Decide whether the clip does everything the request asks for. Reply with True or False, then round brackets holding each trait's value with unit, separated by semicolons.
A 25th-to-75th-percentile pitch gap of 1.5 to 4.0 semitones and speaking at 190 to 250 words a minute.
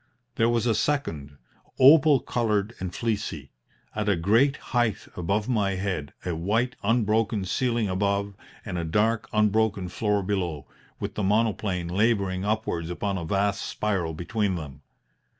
False (3.6 semitones; 145 wpm)